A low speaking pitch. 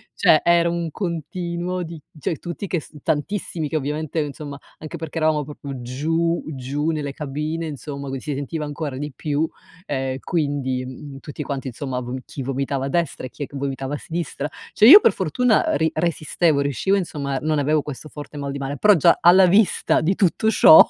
No: medium, 150 Hz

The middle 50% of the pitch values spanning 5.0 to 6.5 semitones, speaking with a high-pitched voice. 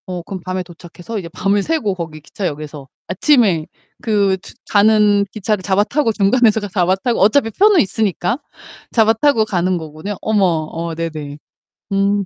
No: average, 3.9 semitones; high, 195 Hz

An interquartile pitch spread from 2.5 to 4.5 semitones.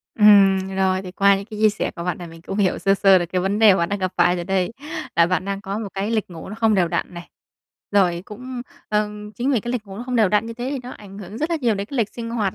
Yes: average, 2.8 semitones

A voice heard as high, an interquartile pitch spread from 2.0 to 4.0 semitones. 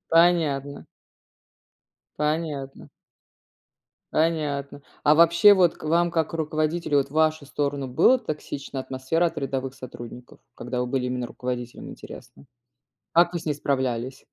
No: medium, 145 Hz; average, 3.7 semitones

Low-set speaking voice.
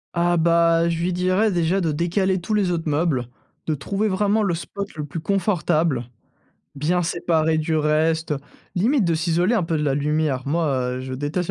No: medium, 170 Hz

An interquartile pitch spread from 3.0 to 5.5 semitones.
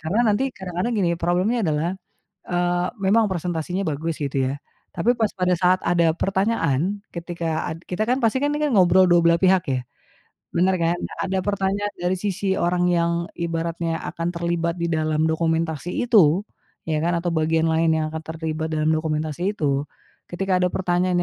No: narrow, 2.6 semitones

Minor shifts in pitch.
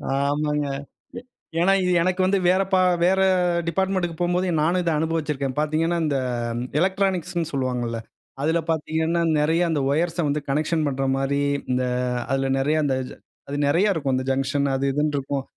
No: average, 3.7 semitones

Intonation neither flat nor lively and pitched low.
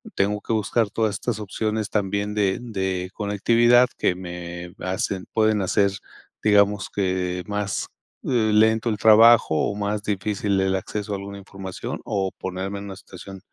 No: narrow, 2.1 semitones; low, 100 Hz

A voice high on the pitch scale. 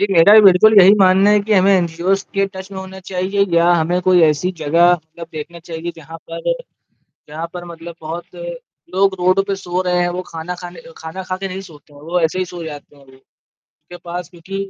No: medium, 175 Hz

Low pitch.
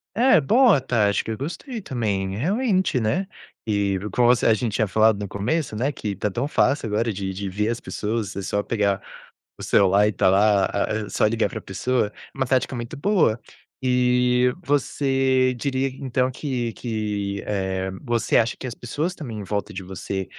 Yes: low, 115 Hz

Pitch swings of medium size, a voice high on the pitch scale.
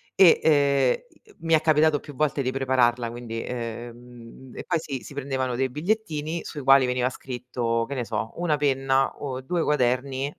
No: average, 3.2 semitones; low, 135 Hz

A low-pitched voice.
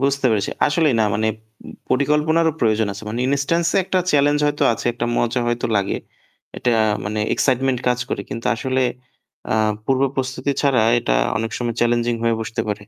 Yes: low, 125 Hz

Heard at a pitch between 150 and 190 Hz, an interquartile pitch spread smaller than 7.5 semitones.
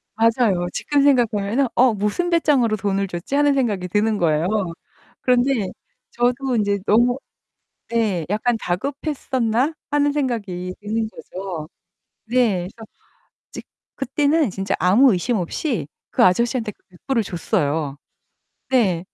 No: high, 225 Hz; wide, 5.5 semitones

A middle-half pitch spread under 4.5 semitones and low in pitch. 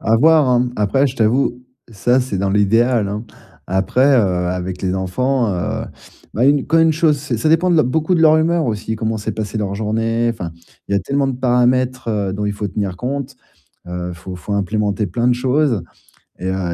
No: average, 4.9 semitones; low, 115 Hz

